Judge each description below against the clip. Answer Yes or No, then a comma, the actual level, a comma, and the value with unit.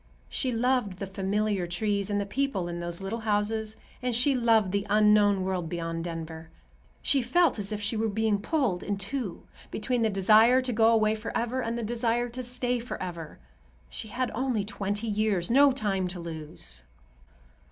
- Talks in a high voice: Yes, high, 215 Hz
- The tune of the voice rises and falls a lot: No, average, 3.6 semitones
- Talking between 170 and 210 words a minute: Yes, average, 175 wpm